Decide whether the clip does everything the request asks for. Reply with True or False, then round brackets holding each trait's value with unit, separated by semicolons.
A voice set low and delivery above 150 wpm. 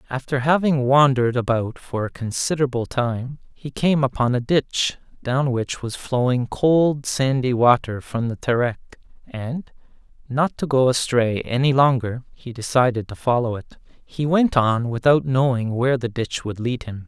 True (125 Hz; 160 wpm)